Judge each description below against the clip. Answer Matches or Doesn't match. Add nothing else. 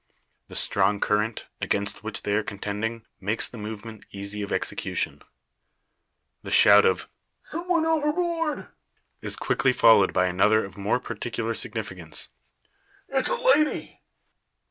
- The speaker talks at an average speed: Doesn't match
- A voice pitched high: Doesn't match